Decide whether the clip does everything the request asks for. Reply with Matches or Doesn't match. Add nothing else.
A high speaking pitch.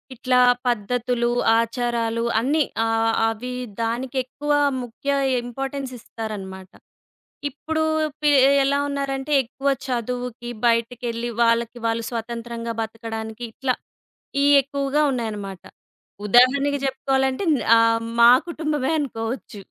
Matches